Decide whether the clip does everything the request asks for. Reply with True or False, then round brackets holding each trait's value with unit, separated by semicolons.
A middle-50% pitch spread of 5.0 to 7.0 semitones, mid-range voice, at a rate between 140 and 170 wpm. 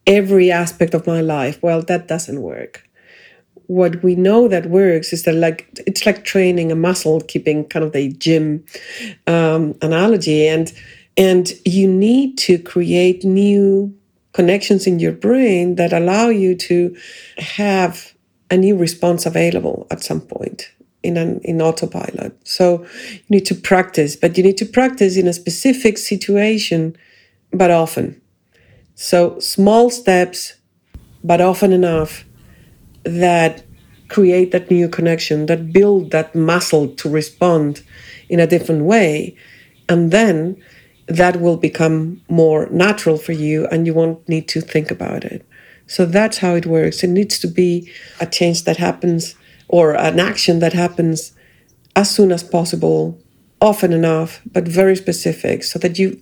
False (2.9 semitones; 175 Hz; 150 wpm)